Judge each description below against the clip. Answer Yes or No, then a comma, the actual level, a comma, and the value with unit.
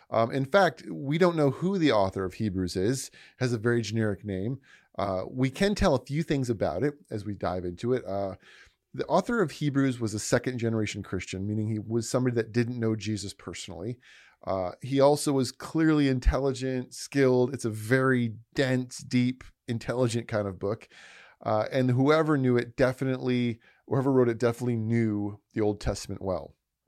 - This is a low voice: Yes, low, 120 Hz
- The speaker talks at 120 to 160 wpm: No, average, 180 wpm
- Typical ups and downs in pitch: Yes, average, 4.1 semitones